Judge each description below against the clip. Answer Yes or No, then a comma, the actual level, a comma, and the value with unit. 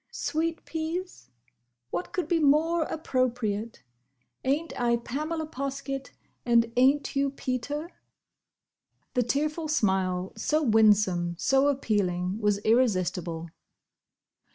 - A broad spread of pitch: Yes, wide, 6.5 semitones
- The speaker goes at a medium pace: No, slow, 100 wpm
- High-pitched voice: Yes, very high, 255 Hz